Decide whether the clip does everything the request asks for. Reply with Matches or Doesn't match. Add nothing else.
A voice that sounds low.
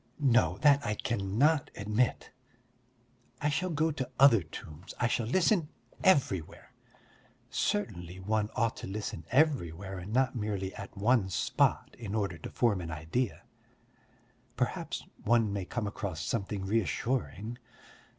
Matches